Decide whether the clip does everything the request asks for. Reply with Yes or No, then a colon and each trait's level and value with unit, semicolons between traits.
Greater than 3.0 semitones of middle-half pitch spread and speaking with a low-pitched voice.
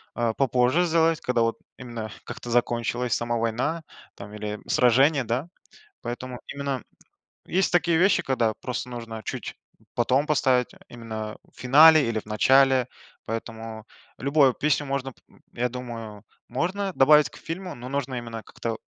Yes: average, 3.5 semitones; low, 125 Hz